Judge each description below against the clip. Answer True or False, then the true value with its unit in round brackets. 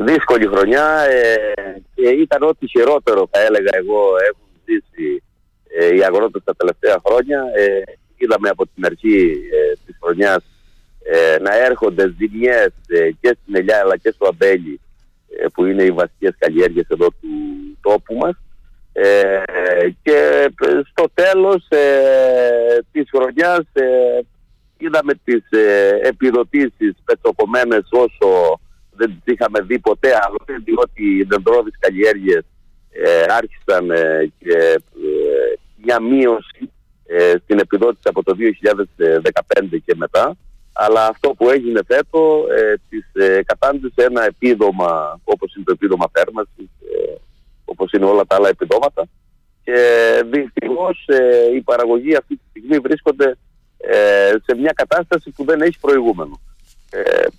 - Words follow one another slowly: False (135 wpm)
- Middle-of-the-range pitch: False (360 Hz)